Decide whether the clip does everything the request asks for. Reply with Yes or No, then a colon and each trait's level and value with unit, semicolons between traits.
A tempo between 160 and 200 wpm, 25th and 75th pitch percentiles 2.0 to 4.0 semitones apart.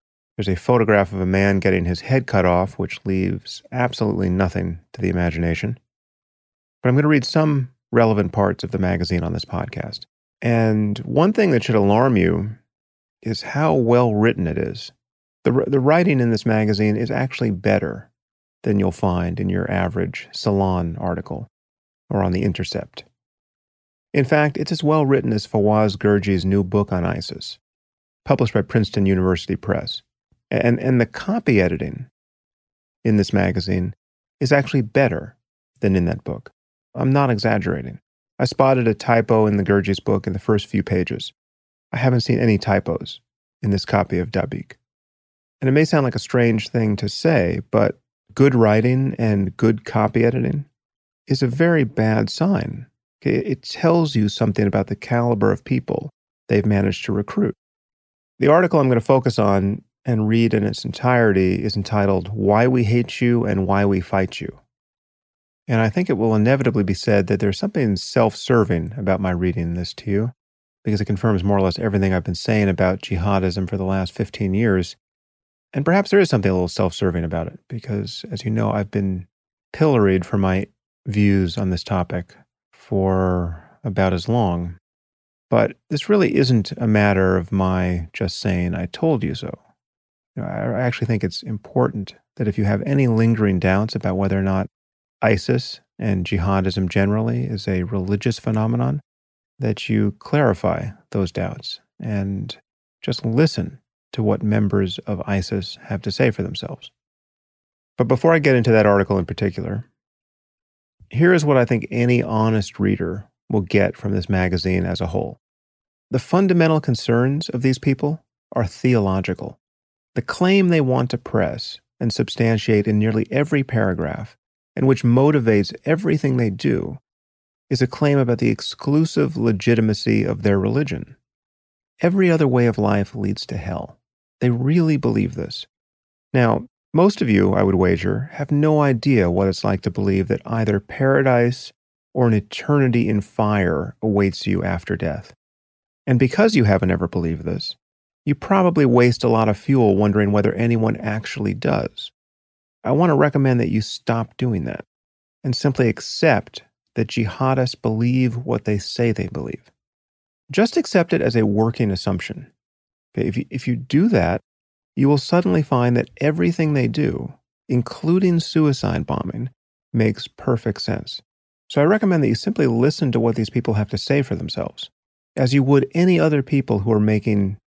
No: average, 165 wpm; average, 4.7 semitones